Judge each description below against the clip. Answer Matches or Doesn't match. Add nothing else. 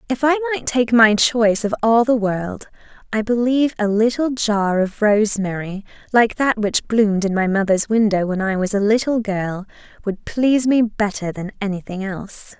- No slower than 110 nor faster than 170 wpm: Doesn't match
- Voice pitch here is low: Doesn't match